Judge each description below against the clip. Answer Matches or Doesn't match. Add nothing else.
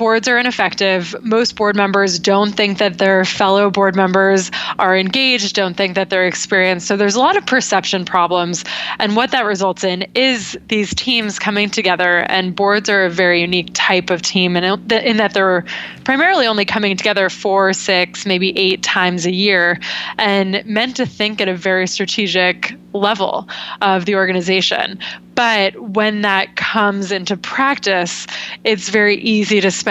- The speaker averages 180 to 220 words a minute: Doesn't match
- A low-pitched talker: Doesn't match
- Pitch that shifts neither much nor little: Doesn't match